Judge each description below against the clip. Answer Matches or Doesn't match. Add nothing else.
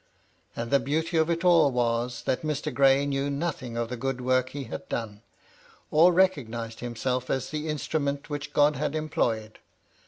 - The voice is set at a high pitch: Doesn't match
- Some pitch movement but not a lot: Matches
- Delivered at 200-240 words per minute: Doesn't match